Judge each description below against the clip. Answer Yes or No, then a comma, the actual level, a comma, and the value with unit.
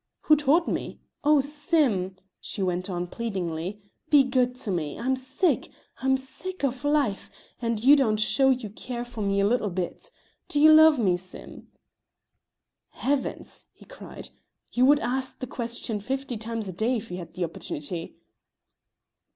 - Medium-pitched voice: No, high, 240 Hz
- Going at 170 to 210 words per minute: No, average, 160 wpm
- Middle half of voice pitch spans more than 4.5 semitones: Yes, wide, 5.6 semitones